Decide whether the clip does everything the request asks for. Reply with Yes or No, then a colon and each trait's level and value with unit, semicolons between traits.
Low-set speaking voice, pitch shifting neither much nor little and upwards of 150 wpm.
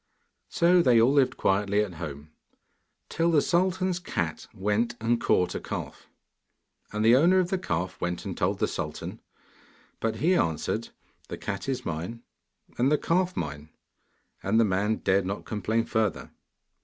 No: low, 110 Hz; wide, 8.1 semitones; average, 160 wpm